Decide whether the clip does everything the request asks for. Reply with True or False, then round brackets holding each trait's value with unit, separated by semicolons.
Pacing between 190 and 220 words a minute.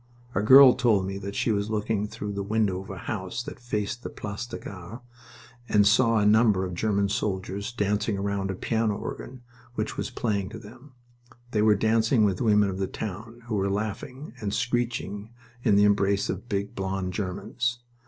True (195 wpm)